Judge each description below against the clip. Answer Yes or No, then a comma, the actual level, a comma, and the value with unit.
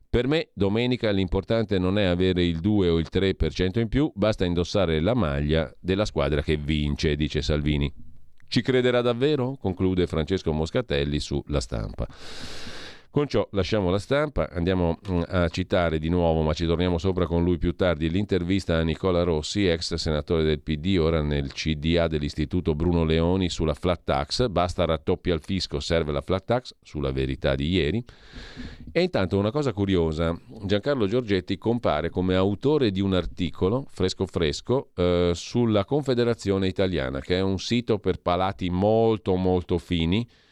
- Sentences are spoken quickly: No, average, 160 wpm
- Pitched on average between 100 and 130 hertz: No, very low, 90 Hz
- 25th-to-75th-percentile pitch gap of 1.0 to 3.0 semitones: No, average, 3.8 semitones